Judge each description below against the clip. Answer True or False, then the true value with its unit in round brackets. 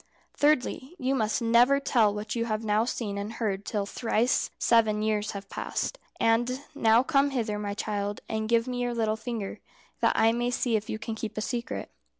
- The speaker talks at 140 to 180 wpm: False (195 wpm)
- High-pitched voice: True (225 Hz)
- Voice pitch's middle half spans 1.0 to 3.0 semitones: True (2.4 semitones)